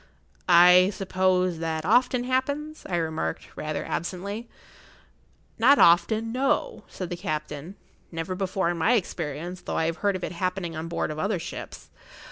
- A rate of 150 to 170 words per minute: Yes, average, 155 wpm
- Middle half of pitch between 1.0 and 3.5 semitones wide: No, average, 4.2 semitones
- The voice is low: No, medium, 180 Hz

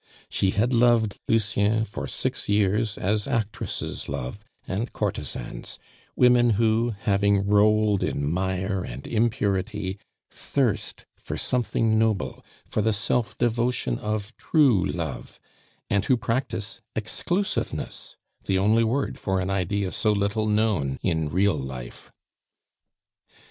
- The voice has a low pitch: Yes, low, 105 Hz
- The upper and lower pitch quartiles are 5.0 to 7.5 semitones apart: No, average, 2.8 semitones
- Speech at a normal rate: No, slow, 120 wpm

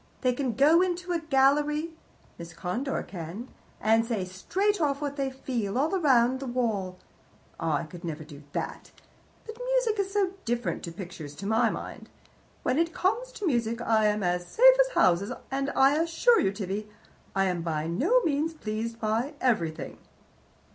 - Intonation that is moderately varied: No, wide, 8.6 semitones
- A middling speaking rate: Yes, average, 175 wpm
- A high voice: Yes, high, 245 Hz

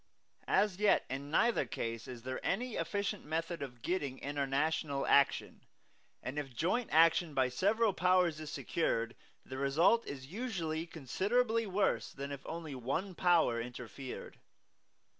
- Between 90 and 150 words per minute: Yes, average, 140 wpm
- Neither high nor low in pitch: Yes, medium, 155 Hz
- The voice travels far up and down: Yes, wide, 5.7 semitones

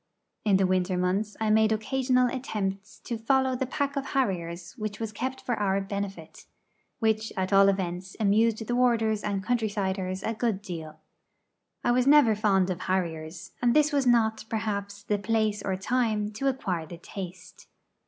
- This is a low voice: No, high, 210 Hz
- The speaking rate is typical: Yes, average, 175 wpm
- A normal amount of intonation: Yes, average, 3.7 semitones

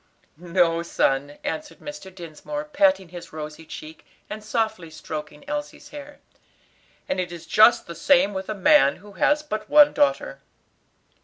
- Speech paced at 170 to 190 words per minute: No, average, 150 wpm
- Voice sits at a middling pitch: No, high, 205 Hz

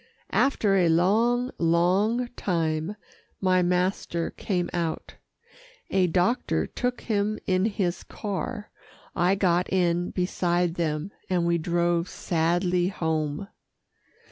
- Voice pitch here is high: No, medium, 180 Hz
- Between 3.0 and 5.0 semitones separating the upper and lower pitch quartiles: No, narrow, 2.6 semitones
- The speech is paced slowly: Yes, slow, 110 wpm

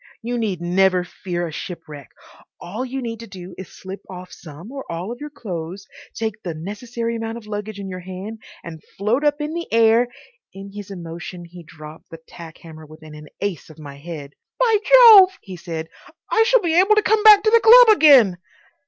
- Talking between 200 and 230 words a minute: Yes, fast, 205 wpm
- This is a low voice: No, high, 195 Hz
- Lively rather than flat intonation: Yes, wide, 6.5 semitones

